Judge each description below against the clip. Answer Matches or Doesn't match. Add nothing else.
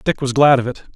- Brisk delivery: Matches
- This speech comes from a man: Matches